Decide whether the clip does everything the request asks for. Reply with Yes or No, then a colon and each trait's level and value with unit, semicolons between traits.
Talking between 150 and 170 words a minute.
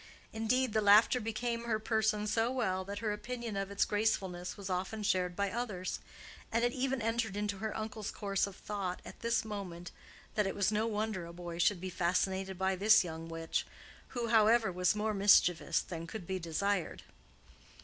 No: average, 180 wpm